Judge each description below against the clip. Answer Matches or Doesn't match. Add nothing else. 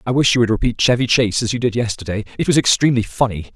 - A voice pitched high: Doesn't match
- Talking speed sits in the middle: Doesn't match